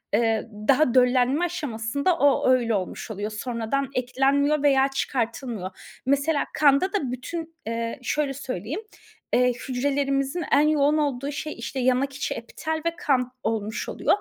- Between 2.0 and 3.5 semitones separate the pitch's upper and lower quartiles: Yes, average, 3.1 semitones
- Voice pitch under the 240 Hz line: No, very high, 270 Hz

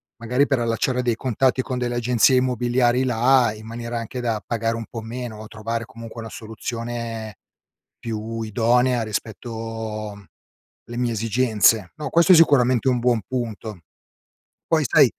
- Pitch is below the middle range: Yes, low, 115 Hz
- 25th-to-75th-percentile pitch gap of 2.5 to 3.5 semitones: No, narrow, 1.8 semitones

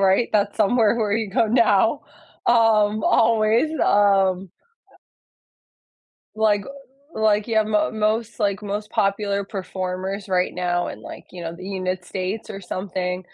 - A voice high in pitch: Yes, high, 205 Hz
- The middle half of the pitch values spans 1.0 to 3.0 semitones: Yes, narrow, 2.5 semitones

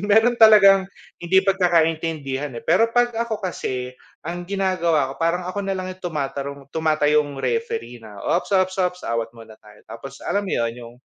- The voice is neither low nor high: Yes, medium, 170 Hz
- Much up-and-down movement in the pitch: Yes, wide, 5.9 semitones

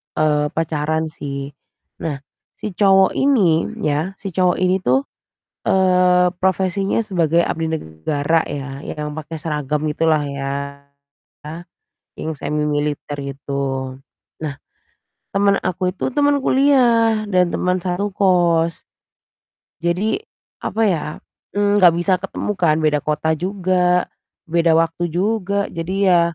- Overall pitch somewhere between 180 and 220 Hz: No, medium, 170 Hz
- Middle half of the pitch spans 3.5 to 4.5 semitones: Yes, average, 4.1 semitones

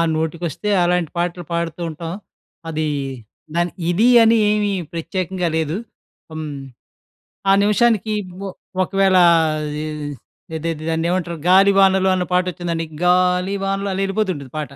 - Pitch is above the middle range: No, medium, 180 Hz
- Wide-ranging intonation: No, average, 2.7 semitones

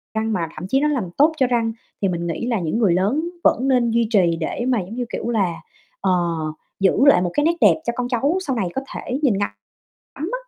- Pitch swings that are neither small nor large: No, wide, 5.9 semitones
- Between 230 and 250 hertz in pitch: Yes, high, 235 Hz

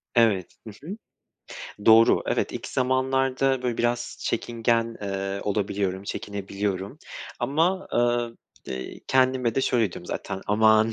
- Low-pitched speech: Yes, low, 115 Hz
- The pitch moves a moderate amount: Yes, average, 4.1 semitones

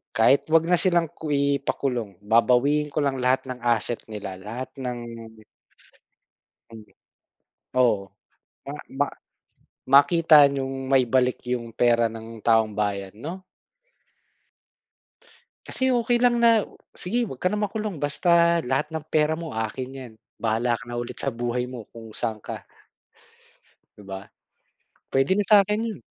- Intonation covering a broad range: Yes, wide, 5.9 semitones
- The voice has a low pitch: Yes, low, 130 Hz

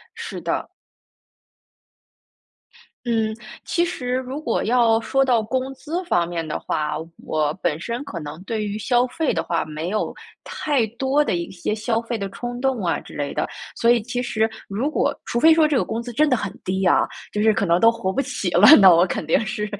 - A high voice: Yes, high, 225 Hz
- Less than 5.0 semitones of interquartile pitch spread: No, wide, 5.4 semitones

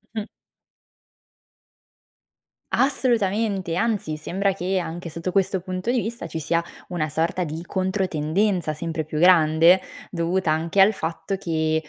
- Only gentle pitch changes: No, average, 3.3 semitones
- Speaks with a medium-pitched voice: Yes, medium, 180 Hz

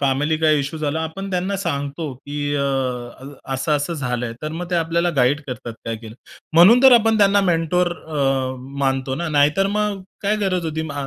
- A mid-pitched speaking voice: Yes, medium, 155 Hz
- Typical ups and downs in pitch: Yes, average, 4.4 semitones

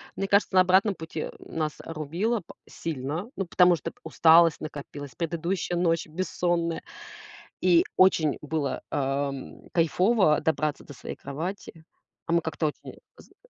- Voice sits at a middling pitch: Yes, medium, 165 Hz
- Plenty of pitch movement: No, average, 2.8 semitones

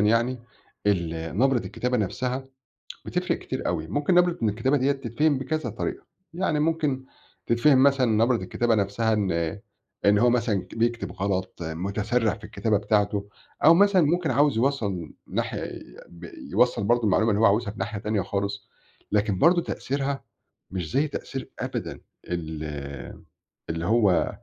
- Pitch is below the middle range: Yes, low, 110 Hz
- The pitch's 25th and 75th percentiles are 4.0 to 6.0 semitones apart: Yes, average, 5.2 semitones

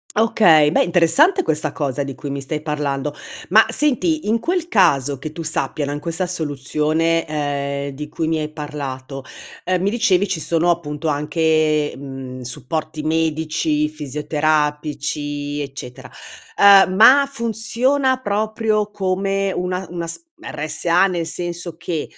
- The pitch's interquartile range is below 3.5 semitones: No, average, 4.5 semitones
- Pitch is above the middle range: No, medium, 160 Hz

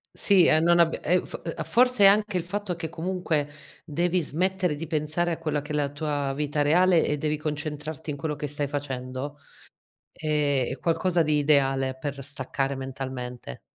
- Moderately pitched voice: Yes, medium, 150 Hz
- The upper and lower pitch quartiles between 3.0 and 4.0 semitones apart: Yes, average, 3.3 semitones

